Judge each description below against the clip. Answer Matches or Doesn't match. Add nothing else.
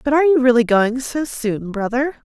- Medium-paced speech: Doesn't match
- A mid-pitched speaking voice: Doesn't match